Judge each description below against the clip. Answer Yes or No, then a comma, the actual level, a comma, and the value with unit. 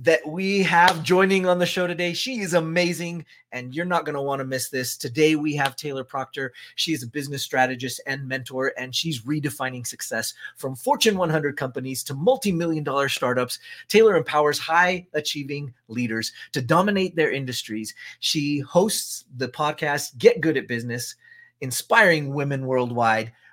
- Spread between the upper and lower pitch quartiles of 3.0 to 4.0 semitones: No, average, 4.8 semitones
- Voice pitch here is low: No, medium, 145 Hz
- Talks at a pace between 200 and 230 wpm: No, average, 160 wpm